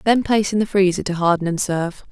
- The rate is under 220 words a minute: No, fast, 255 wpm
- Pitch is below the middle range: No, high, 190 Hz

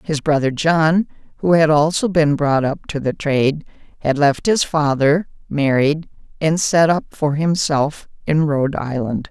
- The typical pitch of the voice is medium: Yes, medium, 150 Hz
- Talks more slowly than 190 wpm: Yes, average, 160 wpm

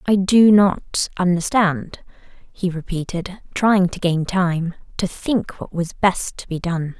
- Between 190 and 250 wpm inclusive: No, average, 155 wpm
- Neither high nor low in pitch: Yes, medium, 180 Hz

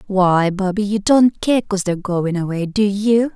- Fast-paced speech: No, average, 195 wpm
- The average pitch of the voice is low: No, high, 200 Hz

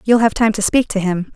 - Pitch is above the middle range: Yes, high, 215 Hz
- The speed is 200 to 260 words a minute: No, fast, 310 wpm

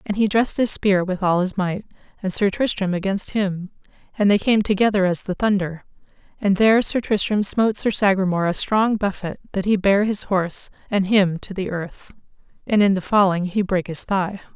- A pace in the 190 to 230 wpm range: Yes, average, 200 wpm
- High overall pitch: Yes, high, 195 Hz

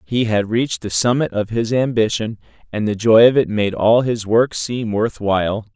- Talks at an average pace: No, fast, 210 wpm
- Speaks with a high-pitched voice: No, low, 110 Hz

